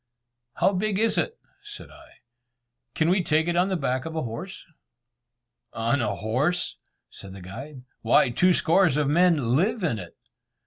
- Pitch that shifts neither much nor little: No, wide, 7.3 semitones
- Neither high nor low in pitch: Yes, medium, 155 Hz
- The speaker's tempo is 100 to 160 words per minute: No, average, 170 wpm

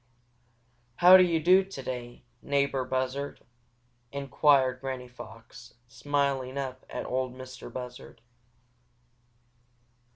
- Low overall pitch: Yes, low, 130 Hz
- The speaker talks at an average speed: No, slow, 95 wpm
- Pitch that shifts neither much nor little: No, narrow, 1.8 semitones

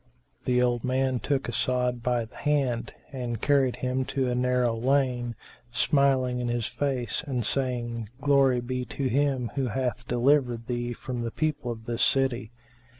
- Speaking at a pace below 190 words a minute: Yes, average, 160 wpm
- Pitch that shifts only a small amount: Yes, narrow, 1.9 semitones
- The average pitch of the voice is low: Yes, low, 125 Hz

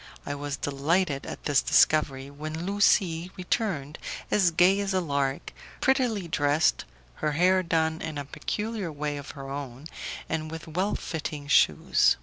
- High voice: No, medium, 160 Hz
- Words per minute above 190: No, average, 150 wpm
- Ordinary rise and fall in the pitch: Yes, average, 4.2 semitones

